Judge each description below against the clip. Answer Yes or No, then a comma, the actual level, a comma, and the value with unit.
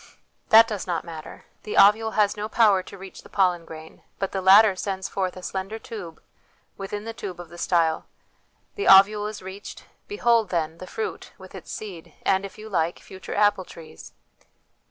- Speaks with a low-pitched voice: No, high, 195 Hz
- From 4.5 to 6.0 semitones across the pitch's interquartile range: No, average, 2.9 semitones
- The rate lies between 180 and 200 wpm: Yes, average, 185 wpm